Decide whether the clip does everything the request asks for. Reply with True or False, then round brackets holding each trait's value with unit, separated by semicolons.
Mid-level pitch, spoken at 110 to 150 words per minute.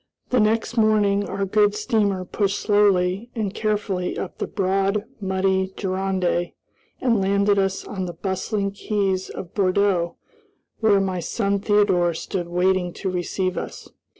False (195 Hz; 140 wpm)